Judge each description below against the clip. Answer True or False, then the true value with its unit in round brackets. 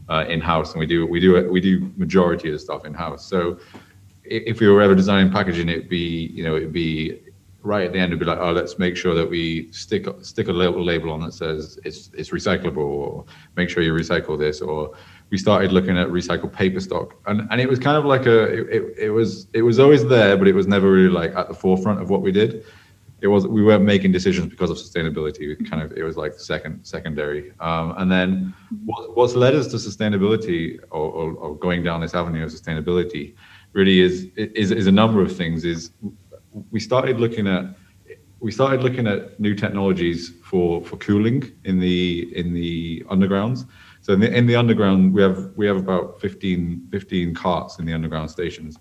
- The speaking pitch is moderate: False (95 Hz)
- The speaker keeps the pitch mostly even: False (3.3 semitones)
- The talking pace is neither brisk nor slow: False (215 wpm)